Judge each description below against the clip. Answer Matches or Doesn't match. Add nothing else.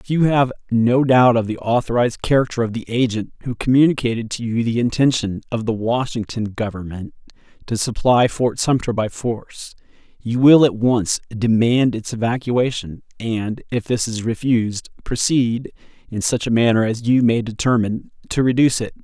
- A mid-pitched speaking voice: Doesn't match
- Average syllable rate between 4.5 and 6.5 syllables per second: Matches